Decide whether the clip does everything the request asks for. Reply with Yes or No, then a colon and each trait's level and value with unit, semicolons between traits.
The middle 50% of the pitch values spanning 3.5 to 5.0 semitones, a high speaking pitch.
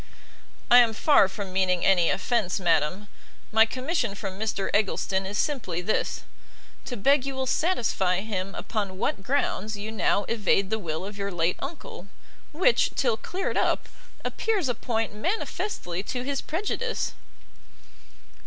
No: wide, 5.5 semitones; high, 215 Hz